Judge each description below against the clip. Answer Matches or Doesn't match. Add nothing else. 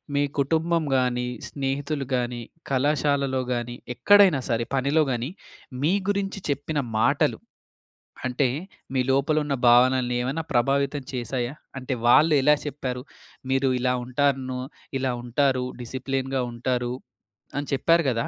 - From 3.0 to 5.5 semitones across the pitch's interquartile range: Doesn't match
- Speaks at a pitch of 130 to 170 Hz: Matches